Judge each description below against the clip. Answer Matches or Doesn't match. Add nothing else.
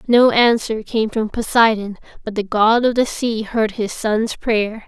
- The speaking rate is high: Doesn't match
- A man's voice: Doesn't match